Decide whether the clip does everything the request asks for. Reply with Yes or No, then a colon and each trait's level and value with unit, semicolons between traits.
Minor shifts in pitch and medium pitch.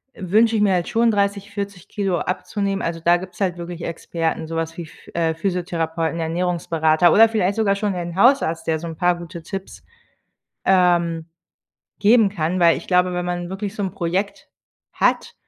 No: average, 3.1 semitones; medium, 180 Hz